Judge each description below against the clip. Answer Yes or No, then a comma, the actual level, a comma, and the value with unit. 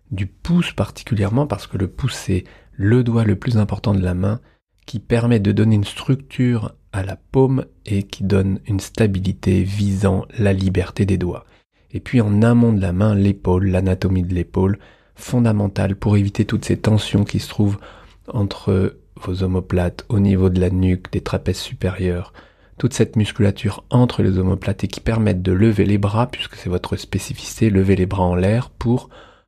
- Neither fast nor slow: Yes, average, 180 wpm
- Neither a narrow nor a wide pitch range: Yes, average, 3.0 semitones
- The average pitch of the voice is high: No, low, 100 Hz